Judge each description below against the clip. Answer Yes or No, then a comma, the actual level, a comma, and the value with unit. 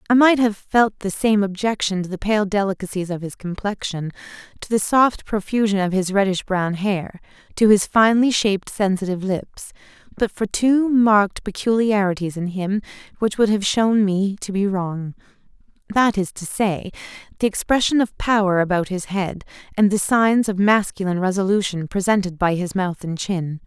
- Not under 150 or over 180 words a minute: Yes, average, 165 wpm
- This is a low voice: No, high, 200 Hz